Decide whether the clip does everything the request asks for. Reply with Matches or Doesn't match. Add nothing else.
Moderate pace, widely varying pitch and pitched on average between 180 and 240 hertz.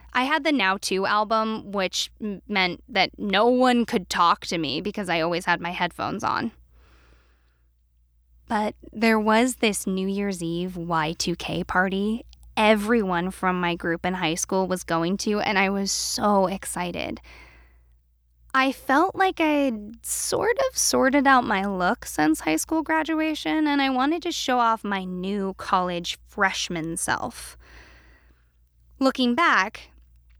Matches